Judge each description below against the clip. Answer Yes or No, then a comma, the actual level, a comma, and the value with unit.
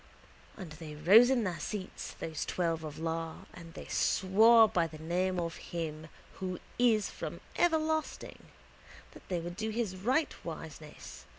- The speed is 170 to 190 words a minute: No, average, 150 wpm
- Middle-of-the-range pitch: Yes, medium, 180 Hz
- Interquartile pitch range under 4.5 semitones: No, average, 5.1 semitones